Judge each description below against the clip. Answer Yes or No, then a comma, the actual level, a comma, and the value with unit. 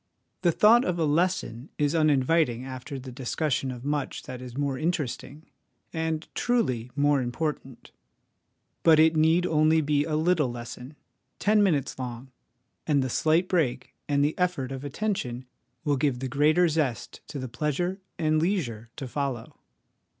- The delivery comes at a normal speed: Yes, average, 155 wpm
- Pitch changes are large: No, average, 3.8 semitones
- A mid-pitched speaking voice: Yes, medium, 145 Hz